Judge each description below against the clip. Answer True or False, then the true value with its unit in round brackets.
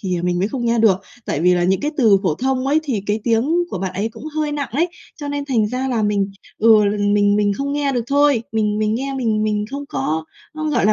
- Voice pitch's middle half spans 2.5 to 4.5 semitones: False (5.2 semitones)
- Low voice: False (225 Hz)